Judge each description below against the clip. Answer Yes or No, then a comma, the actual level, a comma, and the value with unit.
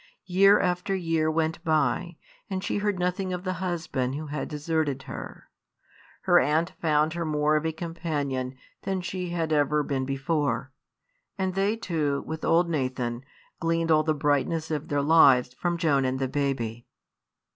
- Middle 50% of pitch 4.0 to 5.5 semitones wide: No, average, 3.6 semitones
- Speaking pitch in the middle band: Yes, medium, 155 Hz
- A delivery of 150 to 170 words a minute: Yes, average, 165 wpm